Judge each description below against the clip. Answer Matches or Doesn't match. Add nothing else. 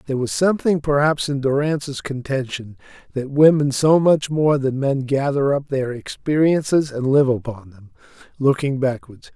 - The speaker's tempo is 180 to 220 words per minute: Doesn't match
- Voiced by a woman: Doesn't match